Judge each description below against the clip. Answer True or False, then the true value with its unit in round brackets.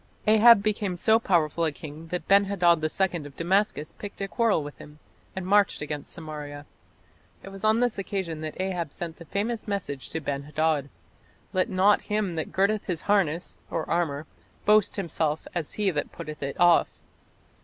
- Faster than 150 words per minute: True (175 wpm)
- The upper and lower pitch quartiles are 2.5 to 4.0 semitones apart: False (4.6 semitones)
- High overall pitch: False (175 Hz)